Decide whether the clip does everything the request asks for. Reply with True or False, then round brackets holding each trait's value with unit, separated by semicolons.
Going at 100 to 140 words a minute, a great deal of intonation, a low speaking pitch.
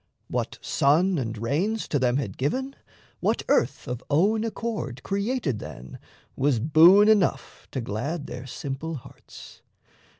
False (135 wpm; 7.9 semitones; 145 Hz)